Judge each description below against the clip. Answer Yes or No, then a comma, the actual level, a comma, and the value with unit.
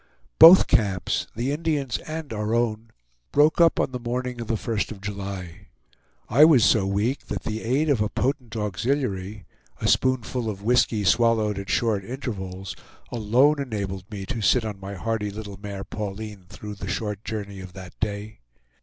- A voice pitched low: Yes, low, 110 Hz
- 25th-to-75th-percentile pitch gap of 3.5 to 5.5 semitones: Yes, average, 3.8 semitones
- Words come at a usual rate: Yes, average, 170 wpm